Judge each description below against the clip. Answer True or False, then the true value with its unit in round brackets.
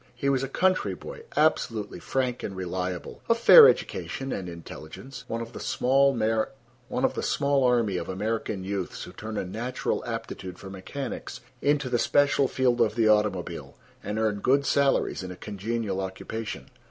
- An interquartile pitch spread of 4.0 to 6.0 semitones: True (5.3 semitones)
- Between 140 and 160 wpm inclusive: True (155 wpm)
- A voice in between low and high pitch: False (115 Hz)